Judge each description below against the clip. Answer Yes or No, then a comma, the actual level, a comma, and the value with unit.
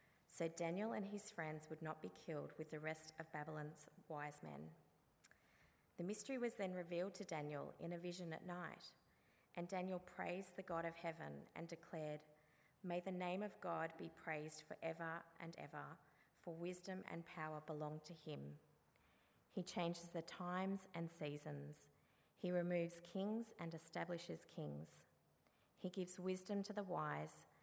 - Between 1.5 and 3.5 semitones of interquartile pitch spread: Yes, average, 2.9 semitones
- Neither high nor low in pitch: Yes, medium, 170 Hz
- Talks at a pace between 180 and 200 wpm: No, average, 155 wpm